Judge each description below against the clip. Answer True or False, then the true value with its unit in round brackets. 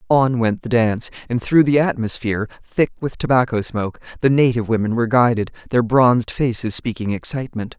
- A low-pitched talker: True (120 Hz)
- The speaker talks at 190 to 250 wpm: False (155 wpm)